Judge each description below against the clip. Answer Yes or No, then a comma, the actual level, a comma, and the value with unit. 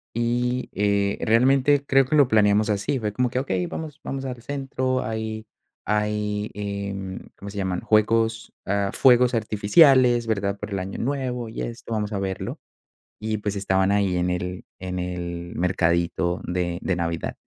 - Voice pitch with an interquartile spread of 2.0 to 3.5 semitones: No, average, 4.3 semitones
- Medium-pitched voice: No, low, 105 Hz